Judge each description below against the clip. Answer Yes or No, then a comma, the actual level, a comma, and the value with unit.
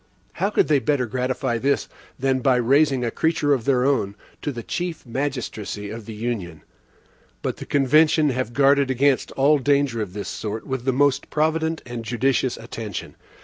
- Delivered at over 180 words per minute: No, average, 175 wpm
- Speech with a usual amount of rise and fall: Yes, average, 3.5 semitones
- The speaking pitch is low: Yes, low, 130 Hz